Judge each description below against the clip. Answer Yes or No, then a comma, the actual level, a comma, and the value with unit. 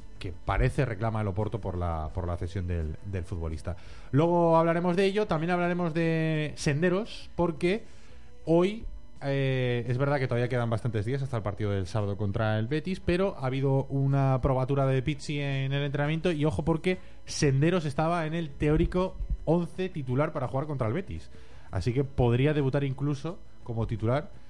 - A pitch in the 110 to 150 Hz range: Yes, low, 135 Hz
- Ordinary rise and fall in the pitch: No, wide, 6.8 semitones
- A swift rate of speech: No, average, 175 wpm